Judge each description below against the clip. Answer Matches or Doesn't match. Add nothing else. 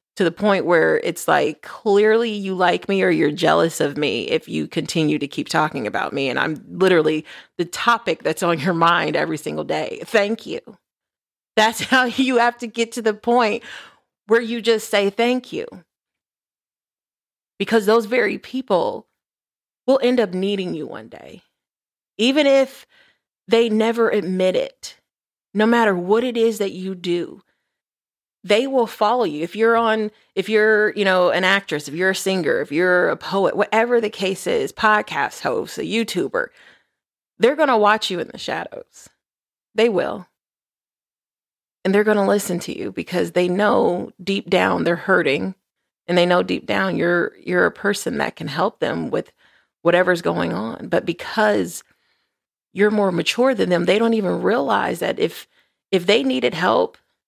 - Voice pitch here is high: Matches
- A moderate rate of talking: Matches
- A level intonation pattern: Doesn't match